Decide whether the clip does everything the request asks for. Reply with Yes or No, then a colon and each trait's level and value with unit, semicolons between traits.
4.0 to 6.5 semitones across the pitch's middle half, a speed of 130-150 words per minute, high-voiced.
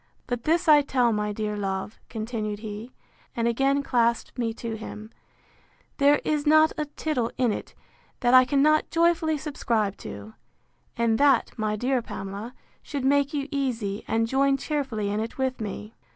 No: average, 4.6 semitones; average, 165 wpm; high, 245 Hz